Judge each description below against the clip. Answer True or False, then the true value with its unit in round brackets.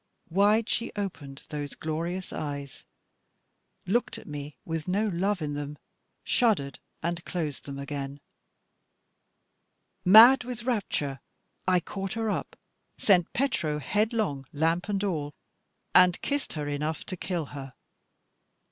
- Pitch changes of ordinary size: False (5.9 semitones)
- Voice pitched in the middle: True (170 Hz)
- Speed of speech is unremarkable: False (125 wpm)